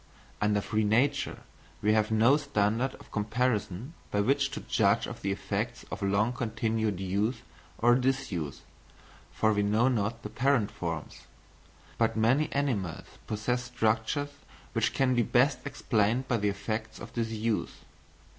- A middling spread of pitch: Yes, average, 3.1 semitones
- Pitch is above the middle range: No, low, 110 Hz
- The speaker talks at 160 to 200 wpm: No, average, 145 wpm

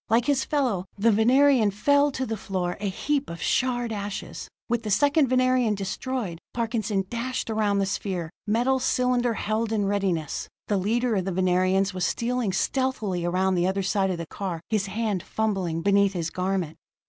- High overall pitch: Yes, high, 205 Hz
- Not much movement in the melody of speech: No, average, 4.3 semitones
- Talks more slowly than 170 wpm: No, average, 175 wpm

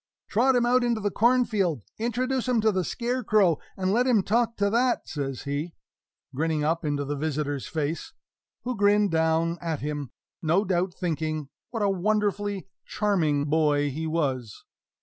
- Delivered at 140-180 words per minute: Yes, average, 160 wpm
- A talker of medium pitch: Yes, medium, 180 Hz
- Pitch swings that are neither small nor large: No, wide, 6.2 semitones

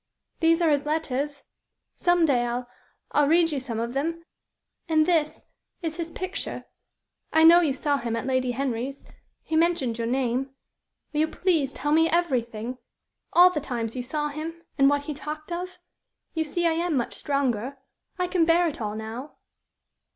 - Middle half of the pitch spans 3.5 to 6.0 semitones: Yes, average, 4.4 semitones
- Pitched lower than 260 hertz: No, very high, 295 Hz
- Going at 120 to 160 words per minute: No, average, 175 wpm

